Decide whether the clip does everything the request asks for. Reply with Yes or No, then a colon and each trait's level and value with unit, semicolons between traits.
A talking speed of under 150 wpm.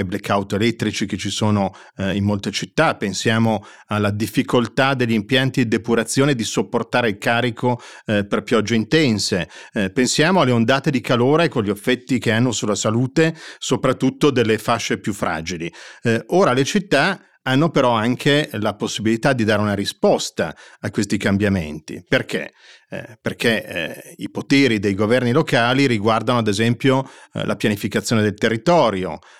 No: average, 155 wpm